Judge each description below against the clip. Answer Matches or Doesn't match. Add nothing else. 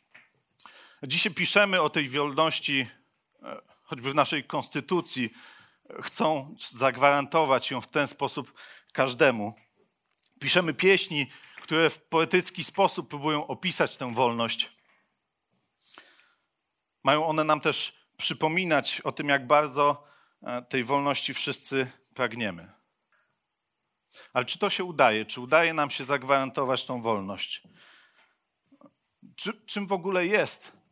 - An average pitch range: Matches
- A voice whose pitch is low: Doesn't match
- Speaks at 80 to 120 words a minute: Matches